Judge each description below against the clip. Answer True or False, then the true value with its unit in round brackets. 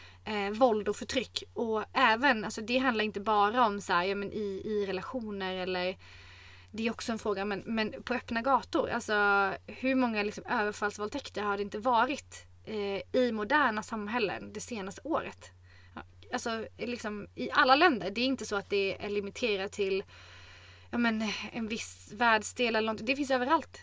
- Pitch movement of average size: True (3.3 semitones)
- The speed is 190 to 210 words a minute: False (175 wpm)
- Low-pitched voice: False (210 Hz)